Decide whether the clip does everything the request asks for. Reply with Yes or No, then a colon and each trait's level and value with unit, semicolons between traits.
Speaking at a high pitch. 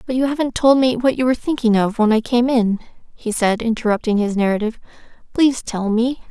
Yes: high, 235 Hz